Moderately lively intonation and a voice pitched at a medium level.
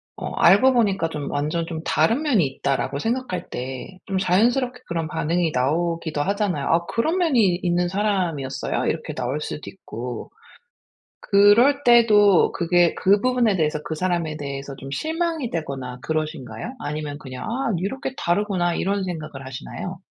No: wide, 6.1 semitones; medium, 175 Hz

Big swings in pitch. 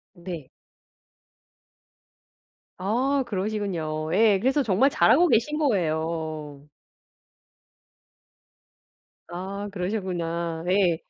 No: average, 5.0 semitones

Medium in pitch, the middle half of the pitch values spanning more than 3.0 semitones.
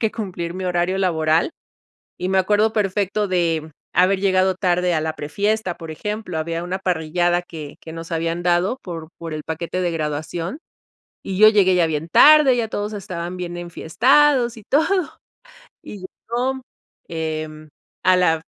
Yes: medium, 180 Hz; average, 3.8 semitones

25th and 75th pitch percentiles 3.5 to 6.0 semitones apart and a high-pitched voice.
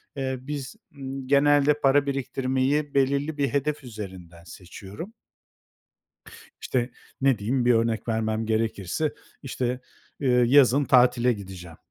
No: average, 3.9 semitones; low, 130 Hz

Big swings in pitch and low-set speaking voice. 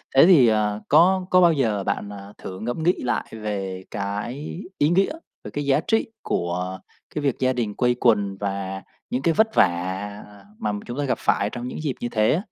Yes: wide, 6.5 semitones; low, 115 Hz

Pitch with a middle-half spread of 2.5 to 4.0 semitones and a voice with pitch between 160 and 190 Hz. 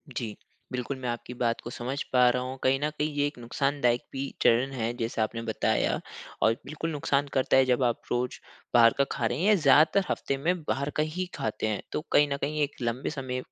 No: average, 3.1 semitones; low, 130 Hz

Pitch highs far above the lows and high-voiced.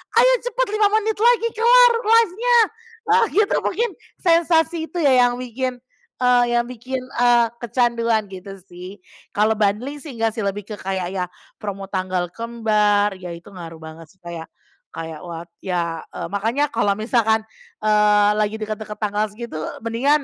Yes: wide, 6.0 semitones; high, 220 Hz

